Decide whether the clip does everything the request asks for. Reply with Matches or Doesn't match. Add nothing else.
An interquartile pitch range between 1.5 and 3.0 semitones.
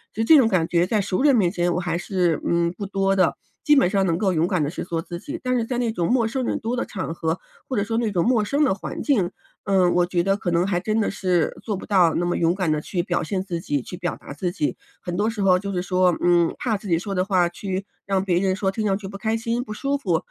Doesn't match